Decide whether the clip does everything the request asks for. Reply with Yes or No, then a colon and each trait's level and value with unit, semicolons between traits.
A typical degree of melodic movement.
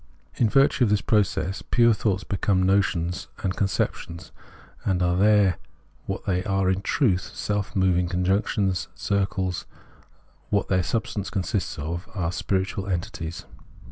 No: narrow, 2.2 semitones